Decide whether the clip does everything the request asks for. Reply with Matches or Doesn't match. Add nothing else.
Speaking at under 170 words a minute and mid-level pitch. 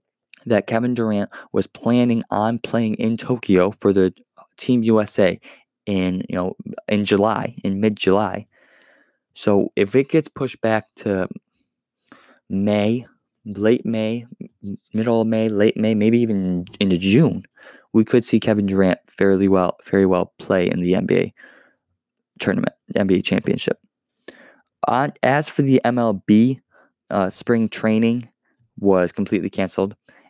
Doesn't match